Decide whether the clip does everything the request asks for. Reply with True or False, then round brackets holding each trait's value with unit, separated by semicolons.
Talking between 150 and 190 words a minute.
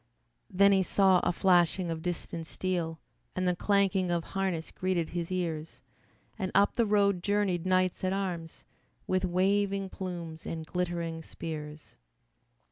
False (140 wpm)